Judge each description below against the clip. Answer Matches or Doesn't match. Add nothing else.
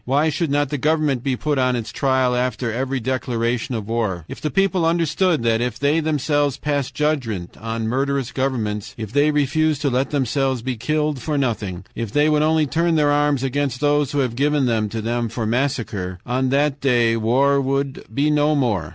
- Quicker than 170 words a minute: Matches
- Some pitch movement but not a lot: Matches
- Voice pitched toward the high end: Doesn't match